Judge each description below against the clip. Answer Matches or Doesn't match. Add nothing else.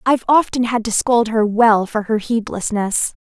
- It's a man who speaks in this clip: Doesn't match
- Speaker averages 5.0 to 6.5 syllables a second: Doesn't match